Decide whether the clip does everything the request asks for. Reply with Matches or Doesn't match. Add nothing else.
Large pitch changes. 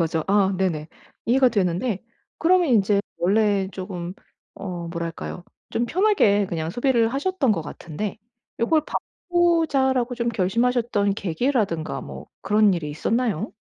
Matches